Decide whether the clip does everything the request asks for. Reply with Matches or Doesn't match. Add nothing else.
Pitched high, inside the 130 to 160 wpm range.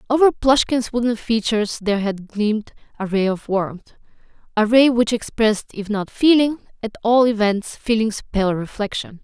Matches